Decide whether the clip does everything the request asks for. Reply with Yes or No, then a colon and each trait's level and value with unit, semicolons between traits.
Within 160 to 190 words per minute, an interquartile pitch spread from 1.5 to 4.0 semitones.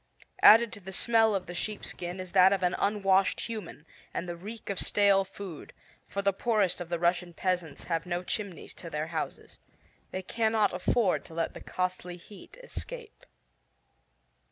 Yes: average, 170 wpm; average, 3.0 semitones